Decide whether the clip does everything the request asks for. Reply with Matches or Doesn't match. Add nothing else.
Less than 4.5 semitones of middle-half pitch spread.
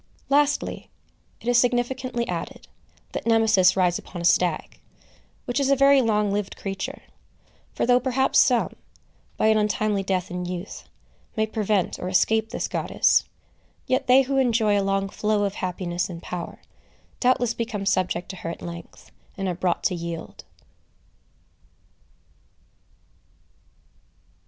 Doesn't match